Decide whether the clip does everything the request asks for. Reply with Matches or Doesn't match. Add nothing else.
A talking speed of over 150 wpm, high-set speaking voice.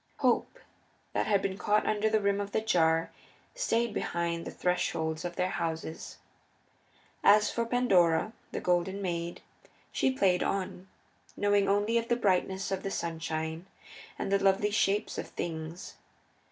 Doesn't match